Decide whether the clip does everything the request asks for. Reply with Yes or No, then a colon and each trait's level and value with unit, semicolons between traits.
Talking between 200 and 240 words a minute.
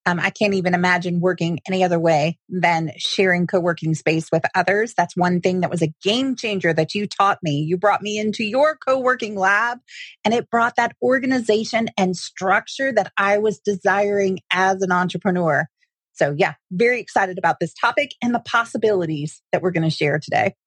No: average, 185 wpm